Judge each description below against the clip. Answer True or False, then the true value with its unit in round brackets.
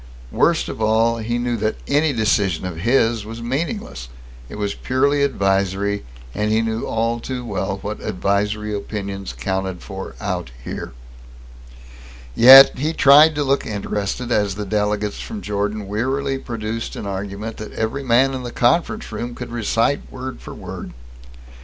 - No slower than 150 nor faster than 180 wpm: True (155 wpm)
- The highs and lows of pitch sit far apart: False (4.0 semitones)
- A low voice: True (110 Hz)